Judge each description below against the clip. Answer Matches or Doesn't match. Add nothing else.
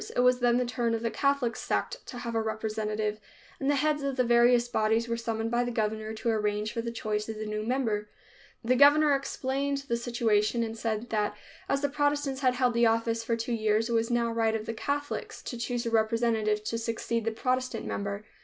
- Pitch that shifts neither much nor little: Doesn't match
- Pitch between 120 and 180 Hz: Doesn't match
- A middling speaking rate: Doesn't match